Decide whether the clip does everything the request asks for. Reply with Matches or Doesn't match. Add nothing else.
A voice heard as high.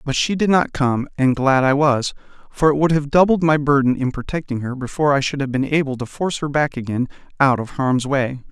Doesn't match